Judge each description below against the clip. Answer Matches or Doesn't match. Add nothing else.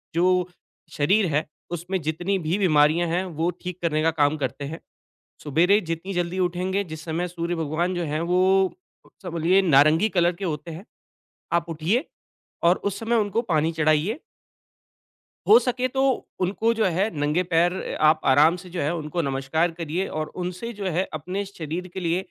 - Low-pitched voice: Doesn't match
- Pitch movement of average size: Matches